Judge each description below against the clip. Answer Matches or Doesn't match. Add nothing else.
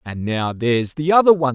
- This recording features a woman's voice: Doesn't match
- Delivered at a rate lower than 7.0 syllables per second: Matches